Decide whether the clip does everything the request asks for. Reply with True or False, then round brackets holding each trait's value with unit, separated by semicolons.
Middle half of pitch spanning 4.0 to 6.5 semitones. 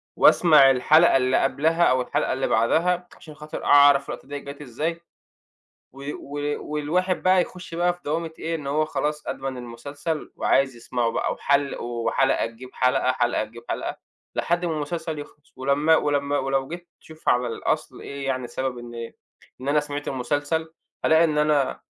False (3.5 semitones)